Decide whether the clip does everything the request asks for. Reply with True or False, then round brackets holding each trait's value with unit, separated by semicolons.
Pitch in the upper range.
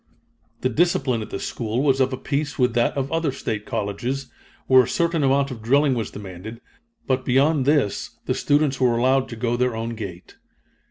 False (130 Hz)